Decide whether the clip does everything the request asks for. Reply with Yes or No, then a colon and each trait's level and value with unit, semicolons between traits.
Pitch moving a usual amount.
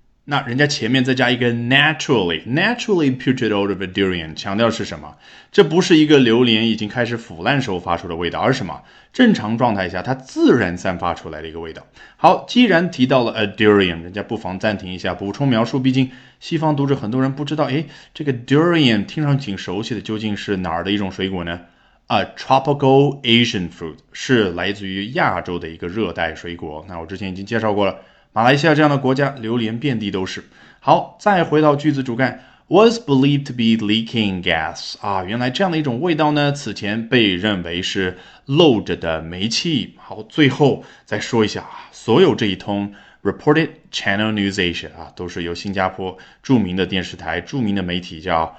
No: wide, 6.5 semitones